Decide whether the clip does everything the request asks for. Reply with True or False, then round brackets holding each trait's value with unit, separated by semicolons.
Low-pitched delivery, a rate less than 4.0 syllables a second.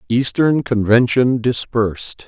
True (120 Hz; 3.8 syllables/s)